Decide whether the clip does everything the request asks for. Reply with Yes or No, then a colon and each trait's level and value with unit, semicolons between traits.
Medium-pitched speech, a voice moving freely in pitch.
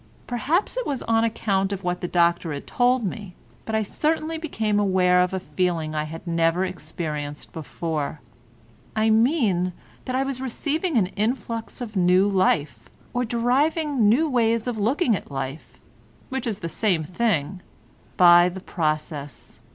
No: high, 200 Hz; wide, 6.0 semitones